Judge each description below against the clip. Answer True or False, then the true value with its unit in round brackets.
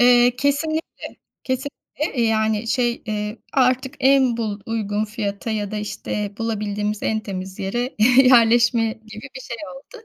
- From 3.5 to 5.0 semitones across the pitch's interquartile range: False (3.1 semitones)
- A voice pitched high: True (225 Hz)